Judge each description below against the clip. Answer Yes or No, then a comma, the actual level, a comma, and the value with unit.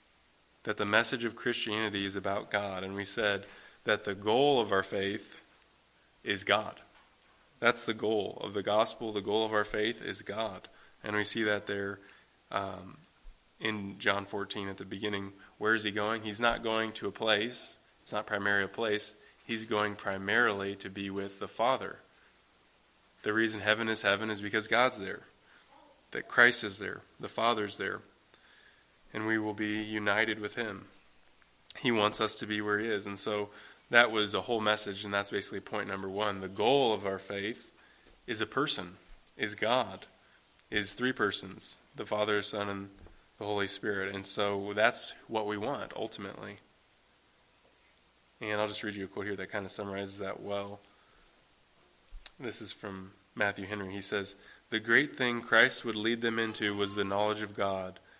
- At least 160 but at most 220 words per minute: Yes, average, 175 wpm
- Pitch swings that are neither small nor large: No, narrow, 1.5 semitones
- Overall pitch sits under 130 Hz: Yes, low, 105 Hz